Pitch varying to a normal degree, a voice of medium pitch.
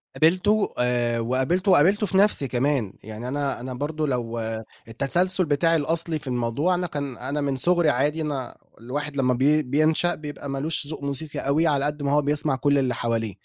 Yes: average, 3.6 semitones; medium, 145 Hz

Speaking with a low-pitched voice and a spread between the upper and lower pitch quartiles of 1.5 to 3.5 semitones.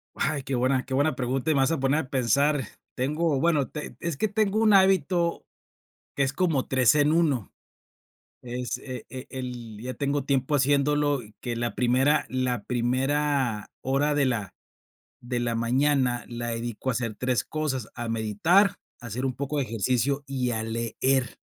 Yes: low, 130 Hz; average, 3.2 semitones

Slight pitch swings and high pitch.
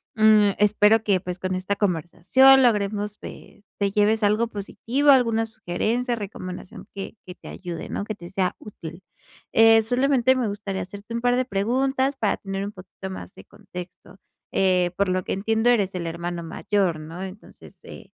No: average, 3.4 semitones; high, 205 Hz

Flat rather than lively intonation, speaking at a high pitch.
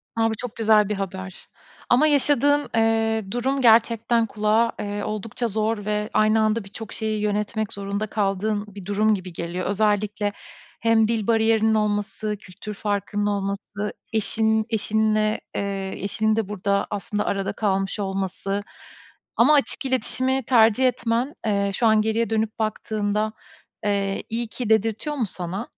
Yes: narrow, 1.8 semitones; high, 215 Hz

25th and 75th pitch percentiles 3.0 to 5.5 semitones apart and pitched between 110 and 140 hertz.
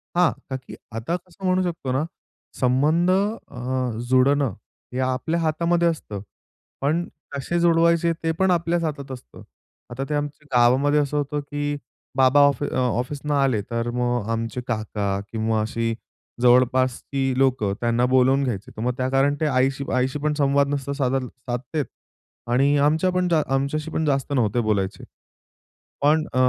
Yes: average, 3.4 semitones; low, 135 Hz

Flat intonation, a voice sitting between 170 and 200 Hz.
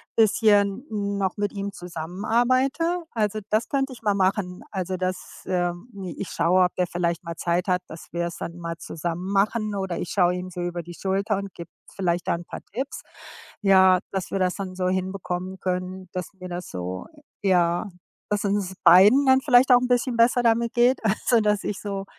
No: average, 3.0 semitones; high, 190 Hz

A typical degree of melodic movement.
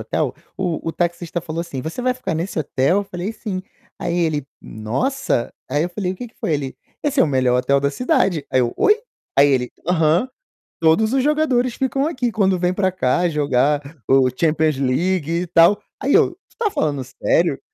No: wide, 6.4 semitones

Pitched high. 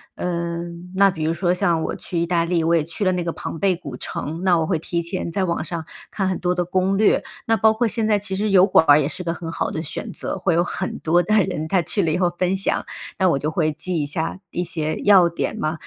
No: medium, 175 Hz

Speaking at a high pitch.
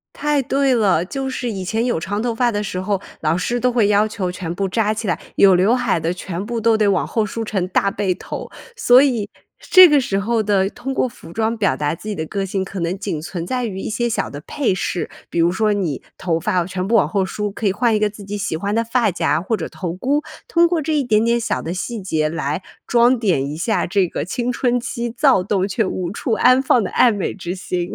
Yes: high, 205 Hz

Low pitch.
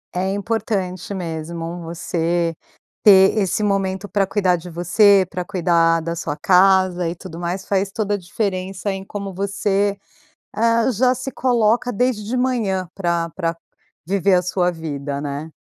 No: high, 190 Hz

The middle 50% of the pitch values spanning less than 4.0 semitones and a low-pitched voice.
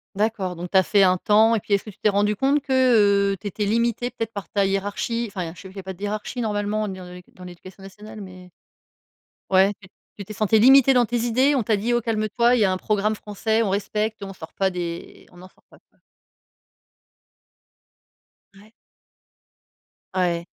No: average, 2.8 semitones; high, 205 Hz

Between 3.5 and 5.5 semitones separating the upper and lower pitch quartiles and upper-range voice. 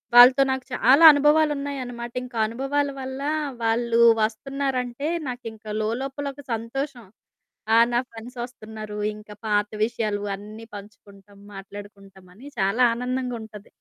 Yes: average, 3.8 semitones; high, 235 Hz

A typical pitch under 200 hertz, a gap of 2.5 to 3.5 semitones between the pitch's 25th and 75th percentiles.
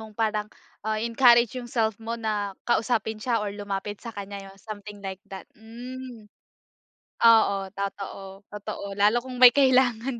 No: high, 220 Hz; average, 2.8 semitones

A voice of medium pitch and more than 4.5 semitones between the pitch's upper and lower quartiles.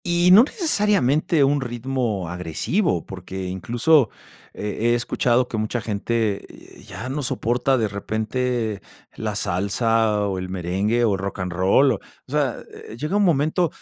No: low, 115 Hz; wide, 5.4 semitones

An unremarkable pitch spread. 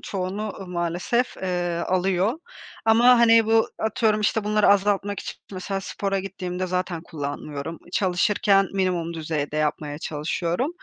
Yes: average, 3.5 semitones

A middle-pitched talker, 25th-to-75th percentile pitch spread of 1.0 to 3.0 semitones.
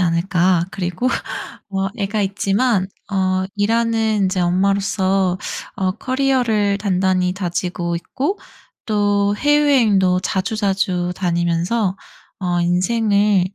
No: high, 195 Hz; average, 2.7 semitones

